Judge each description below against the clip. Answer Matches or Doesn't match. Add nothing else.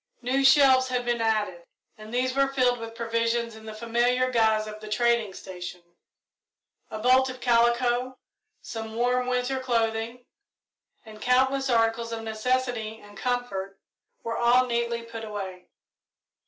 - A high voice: Matches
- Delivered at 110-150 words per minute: Matches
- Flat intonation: Matches